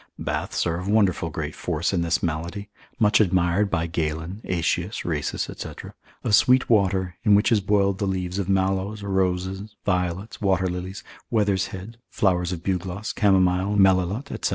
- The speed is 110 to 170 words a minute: Yes, average, 160 wpm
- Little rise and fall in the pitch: Yes, narrow, 2.3 semitones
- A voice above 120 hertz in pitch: No, very low, 95 Hz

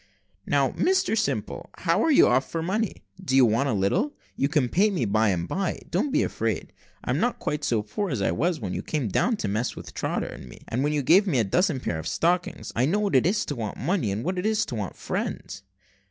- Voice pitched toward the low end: No, medium, 145 Hz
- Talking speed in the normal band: No, fast, 255 wpm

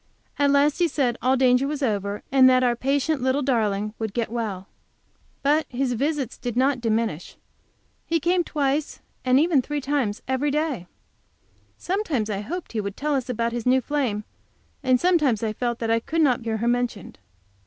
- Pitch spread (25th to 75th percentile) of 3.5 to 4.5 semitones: Yes, average, 4.0 semitones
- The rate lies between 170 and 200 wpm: Yes, average, 180 wpm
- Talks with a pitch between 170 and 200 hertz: No, very high, 255 Hz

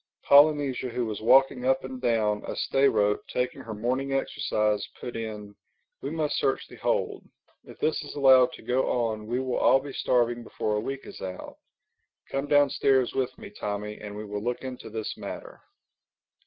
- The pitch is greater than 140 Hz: No, low, 125 Hz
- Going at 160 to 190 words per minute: Yes, average, 180 wpm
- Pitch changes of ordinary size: Yes, average, 3.9 semitones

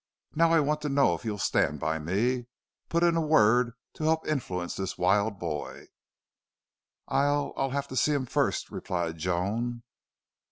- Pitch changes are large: Yes, wide, 8.0 semitones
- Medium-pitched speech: No, low, 120 Hz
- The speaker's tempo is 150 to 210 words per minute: Yes, average, 165 wpm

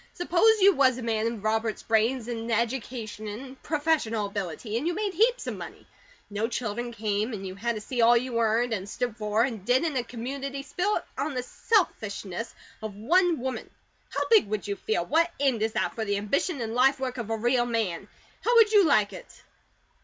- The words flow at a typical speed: No, fast, 210 wpm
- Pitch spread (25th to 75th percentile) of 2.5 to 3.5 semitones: No, average, 4.2 semitones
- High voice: Yes, high, 235 Hz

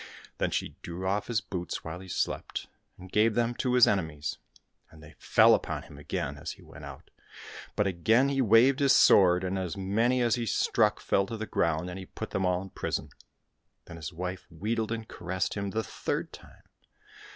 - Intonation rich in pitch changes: No, average, 4.3 semitones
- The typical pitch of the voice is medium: No, very low, 95 Hz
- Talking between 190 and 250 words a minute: Yes, average, 200 wpm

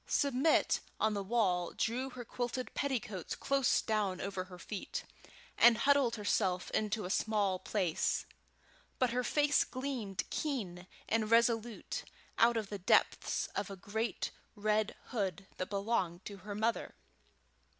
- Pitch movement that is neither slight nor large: Yes, average, 3.6 semitones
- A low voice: No, high, 215 Hz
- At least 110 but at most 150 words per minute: Yes, average, 140 wpm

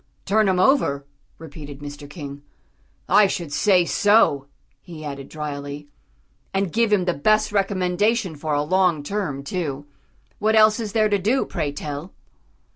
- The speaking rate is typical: Yes, average, 155 wpm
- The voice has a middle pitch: Yes, medium, 175 Hz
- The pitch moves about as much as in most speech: No, wide, 6.1 semitones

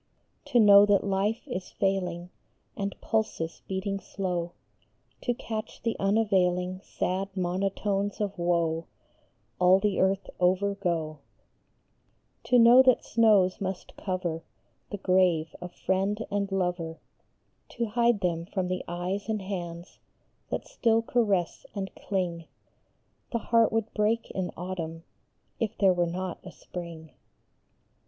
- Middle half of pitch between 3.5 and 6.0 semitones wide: No, average, 2.7 semitones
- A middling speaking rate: No, slow, 130 wpm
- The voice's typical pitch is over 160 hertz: Yes, high, 190 Hz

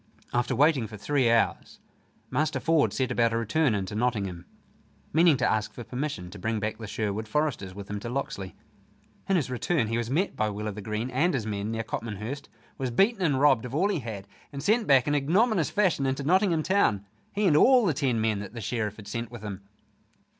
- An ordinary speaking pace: No, fast, 220 wpm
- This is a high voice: No, low, 120 Hz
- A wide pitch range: Yes, wide, 5.9 semitones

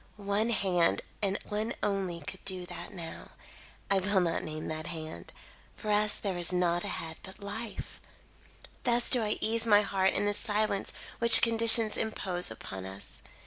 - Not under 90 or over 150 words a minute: No, average, 165 wpm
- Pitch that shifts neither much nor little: Yes, average, 3.4 semitones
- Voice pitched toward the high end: Yes, high, 195 Hz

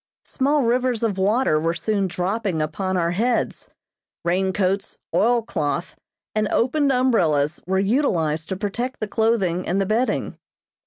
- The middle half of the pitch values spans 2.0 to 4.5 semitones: No, average, 4.9 semitones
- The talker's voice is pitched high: Yes, high, 195 Hz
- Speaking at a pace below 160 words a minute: Yes, average, 145 wpm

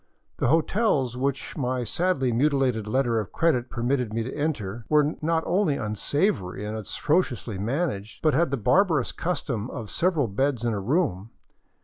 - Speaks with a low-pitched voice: Yes, low, 130 Hz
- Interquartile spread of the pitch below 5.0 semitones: No, wide, 5.5 semitones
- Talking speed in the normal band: Yes, average, 155 wpm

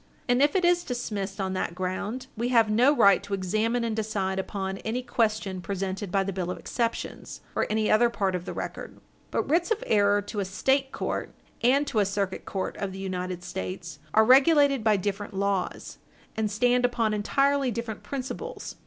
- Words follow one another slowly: No, average, 190 wpm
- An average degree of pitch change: Yes, average, 4.2 semitones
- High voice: Yes, high, 215 Hz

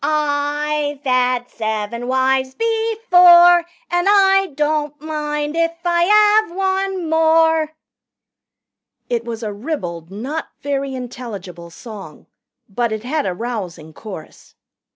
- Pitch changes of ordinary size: No, wide, 6.1 semitones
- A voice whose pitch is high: Yes, very high, 290 Hz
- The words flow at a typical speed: No, slow, 115 wpm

